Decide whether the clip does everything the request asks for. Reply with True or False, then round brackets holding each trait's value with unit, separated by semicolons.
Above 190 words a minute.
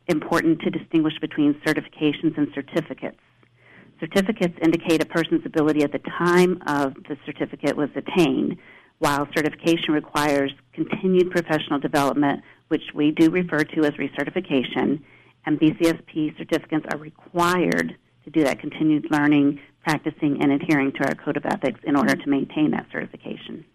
False (145 wpm)